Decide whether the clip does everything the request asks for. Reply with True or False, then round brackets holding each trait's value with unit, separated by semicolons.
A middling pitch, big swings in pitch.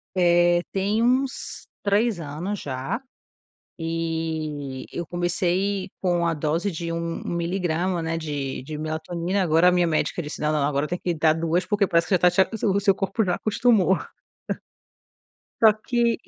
False (175 Hz; 3.3 semitones)